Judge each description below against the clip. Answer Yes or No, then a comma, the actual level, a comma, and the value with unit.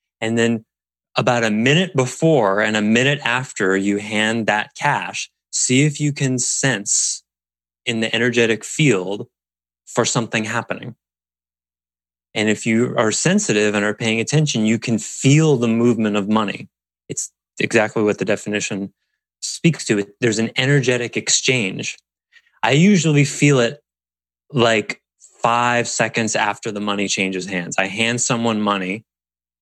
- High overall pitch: No, low, 110 Hz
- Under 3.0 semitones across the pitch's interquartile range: No, average, 3.8 semitones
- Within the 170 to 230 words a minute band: No, average, 140 wpm